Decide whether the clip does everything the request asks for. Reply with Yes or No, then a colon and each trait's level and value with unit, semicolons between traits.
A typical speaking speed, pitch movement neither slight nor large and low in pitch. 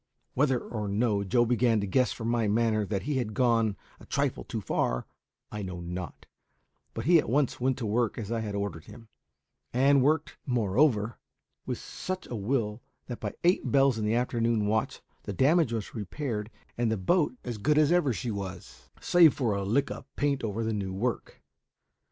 Yes: average, 195 wpm; average, 4.1 semitones; low, 115 Hz